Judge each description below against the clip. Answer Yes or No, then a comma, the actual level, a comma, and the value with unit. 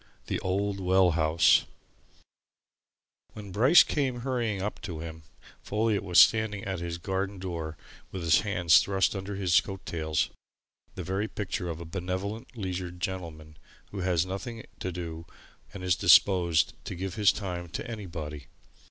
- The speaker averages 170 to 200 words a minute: No, average, 150 wpm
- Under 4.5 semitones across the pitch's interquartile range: Yes, average, 2.9 semitones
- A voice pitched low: Yes, very low, 95 Hz